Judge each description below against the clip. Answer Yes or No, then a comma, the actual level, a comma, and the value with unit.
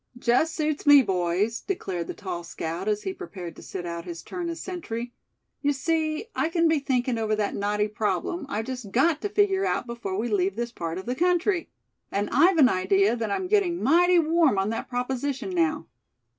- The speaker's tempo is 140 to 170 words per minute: No, average, 200 wpm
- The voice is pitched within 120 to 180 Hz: No, very high, 250 Hz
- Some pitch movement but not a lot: No, wide, 8.4 semitones